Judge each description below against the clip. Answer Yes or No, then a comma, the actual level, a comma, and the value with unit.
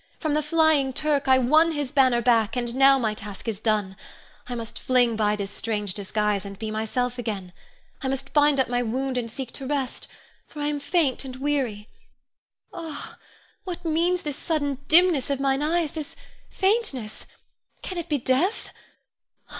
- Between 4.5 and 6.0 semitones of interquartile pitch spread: Yes, average, 4.8 semitones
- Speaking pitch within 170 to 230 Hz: No, very high, 265 Hz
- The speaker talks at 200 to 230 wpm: No, average, 175 wpm